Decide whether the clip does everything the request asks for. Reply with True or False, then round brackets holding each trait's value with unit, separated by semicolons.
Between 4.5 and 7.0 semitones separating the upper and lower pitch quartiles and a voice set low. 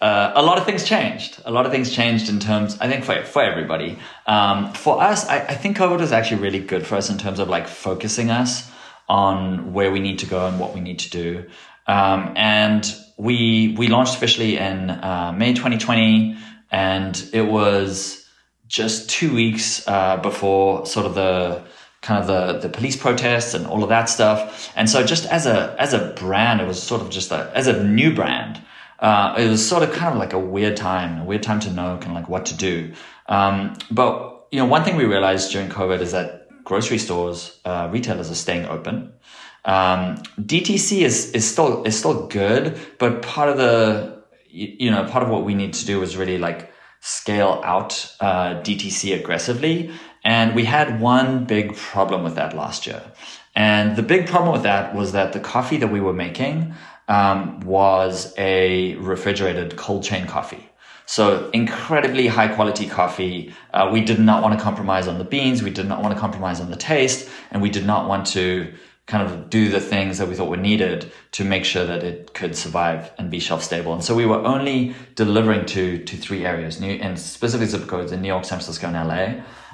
False (3.5 semitones; 100 Hz)